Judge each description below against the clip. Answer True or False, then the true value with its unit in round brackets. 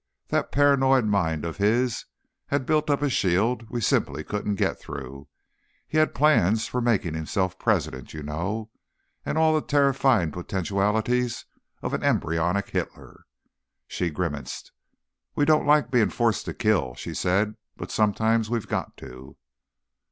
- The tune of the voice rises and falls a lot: True (6.2 semitones)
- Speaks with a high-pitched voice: False (105 Hz)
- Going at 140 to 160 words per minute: True (145 wpm)